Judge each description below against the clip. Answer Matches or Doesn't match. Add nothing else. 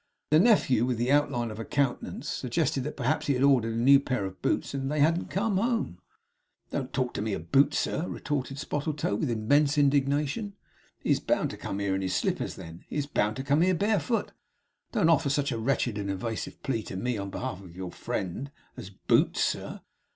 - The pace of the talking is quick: Matches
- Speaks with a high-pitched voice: Doesn't match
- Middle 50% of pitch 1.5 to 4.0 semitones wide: Doesn't match